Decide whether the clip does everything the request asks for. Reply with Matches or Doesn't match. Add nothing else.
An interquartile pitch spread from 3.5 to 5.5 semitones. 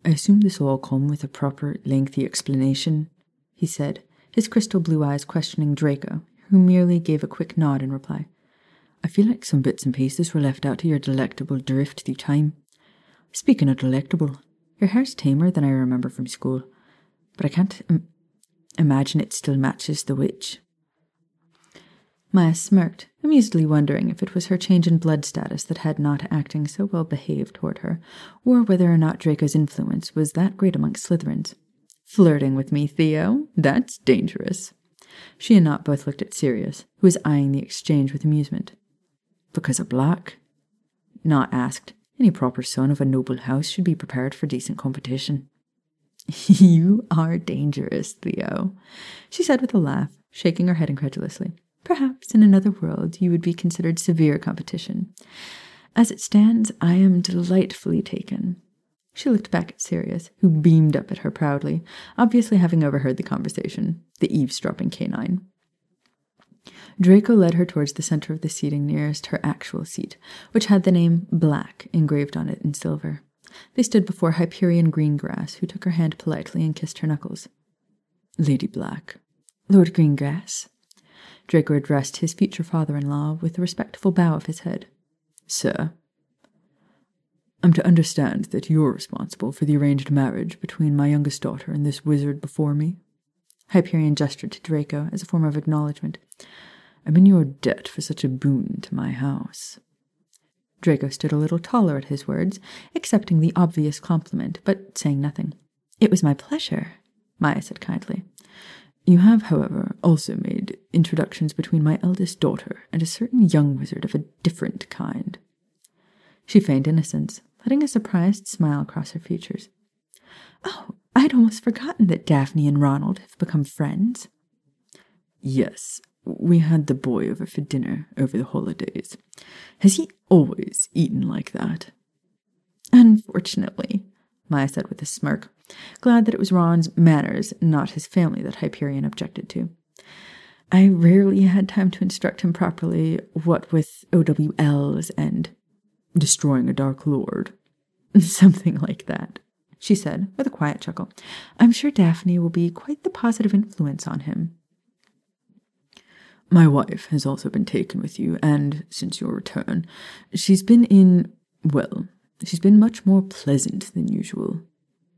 Matches